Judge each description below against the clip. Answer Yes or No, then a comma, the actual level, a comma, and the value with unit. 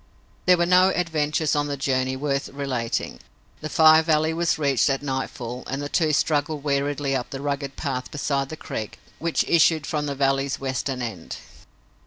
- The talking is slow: No, average, 175 wpm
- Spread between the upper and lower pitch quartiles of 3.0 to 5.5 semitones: No, narrow, 2.5 semitones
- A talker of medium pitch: Yes, medium, 145 Hz